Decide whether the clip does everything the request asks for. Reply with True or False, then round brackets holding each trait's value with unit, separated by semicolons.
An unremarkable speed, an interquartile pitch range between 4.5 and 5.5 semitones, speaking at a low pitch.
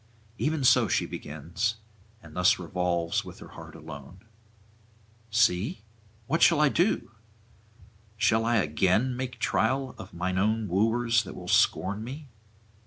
False (130 wpm; 5.2 semitones; 110 Hz)